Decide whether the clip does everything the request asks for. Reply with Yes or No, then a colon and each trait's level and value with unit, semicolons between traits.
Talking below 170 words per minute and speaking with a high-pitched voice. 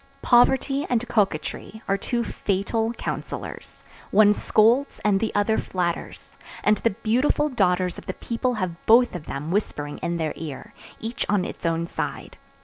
Yes: average, 155 wpm; high, 210 Hz